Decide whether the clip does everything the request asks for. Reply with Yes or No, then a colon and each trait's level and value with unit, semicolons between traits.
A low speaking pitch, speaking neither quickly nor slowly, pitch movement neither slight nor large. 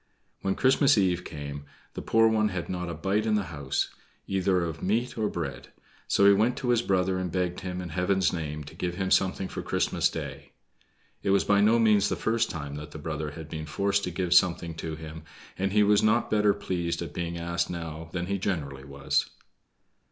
No: very low, 90 Hz; fast, 210 wpm; average, 3.8 semitones